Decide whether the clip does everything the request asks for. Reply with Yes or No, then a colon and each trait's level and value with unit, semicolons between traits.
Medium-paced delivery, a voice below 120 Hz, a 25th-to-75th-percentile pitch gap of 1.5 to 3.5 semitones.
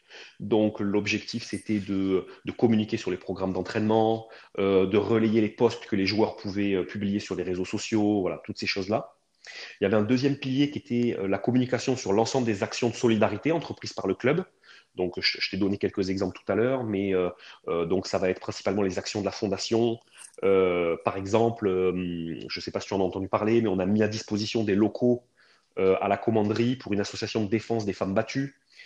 No: fast, 225 wpm; low, 105 Hz; average, 2.9 semitones